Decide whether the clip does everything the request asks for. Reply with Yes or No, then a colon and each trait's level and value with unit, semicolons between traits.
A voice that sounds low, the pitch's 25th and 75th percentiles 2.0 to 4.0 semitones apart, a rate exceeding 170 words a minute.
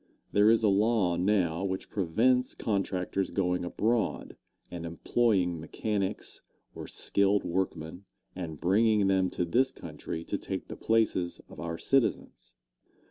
No: very low, 95 Hz; average, 3.7 semitones; slow, 135 wpm